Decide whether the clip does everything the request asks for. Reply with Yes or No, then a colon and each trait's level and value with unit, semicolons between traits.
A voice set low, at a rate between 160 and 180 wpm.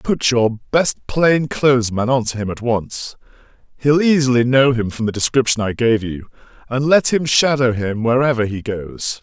Yes: low, 125 Hz; average, 170 wpm